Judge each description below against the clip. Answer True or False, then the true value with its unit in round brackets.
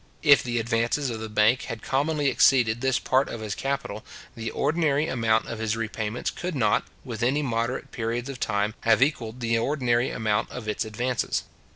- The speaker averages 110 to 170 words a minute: False (180 wpm)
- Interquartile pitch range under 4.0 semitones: True (3.1 semitones)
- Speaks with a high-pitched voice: False (120 Hz)